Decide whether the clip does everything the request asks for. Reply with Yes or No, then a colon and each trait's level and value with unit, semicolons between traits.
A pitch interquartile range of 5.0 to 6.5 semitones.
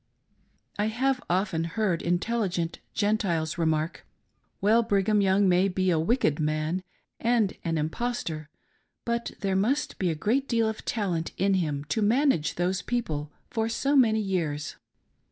Yes: average, 5.3 semitones